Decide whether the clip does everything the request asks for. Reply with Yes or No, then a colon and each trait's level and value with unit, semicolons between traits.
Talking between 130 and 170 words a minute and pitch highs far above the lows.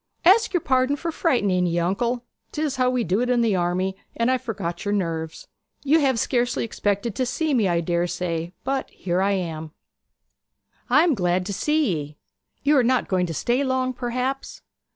No: average, 190 wpm; wide, 6.4 semitones